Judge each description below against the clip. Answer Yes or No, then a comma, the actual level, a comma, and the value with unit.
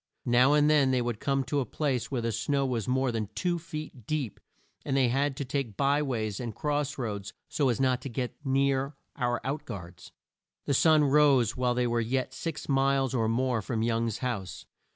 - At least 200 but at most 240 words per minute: Yes, fast, 205 wpm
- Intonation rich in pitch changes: No, average, 3.0 semitones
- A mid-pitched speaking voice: No, low, 130 Hz